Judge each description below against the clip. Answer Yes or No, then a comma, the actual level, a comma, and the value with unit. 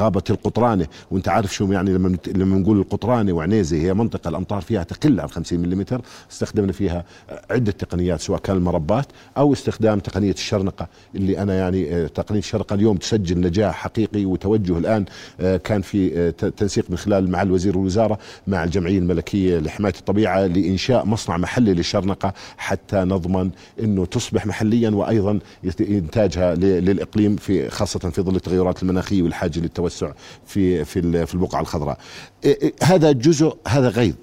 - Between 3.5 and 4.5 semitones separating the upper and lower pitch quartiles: No, average, 2.8 semitones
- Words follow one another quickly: Yes, fast, 150 wpm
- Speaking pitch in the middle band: No, very low, 95 Hz